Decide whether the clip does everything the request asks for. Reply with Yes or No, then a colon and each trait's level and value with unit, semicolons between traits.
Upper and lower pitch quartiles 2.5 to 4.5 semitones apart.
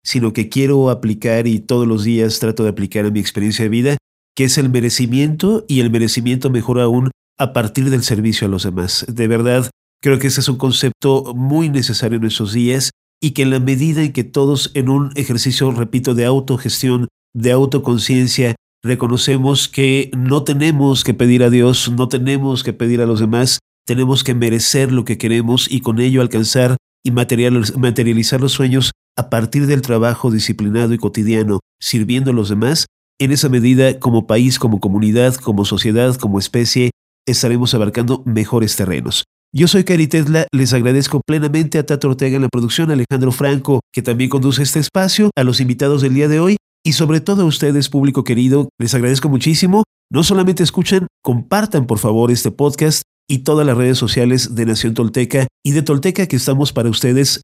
Yes: average, 2.8 semitones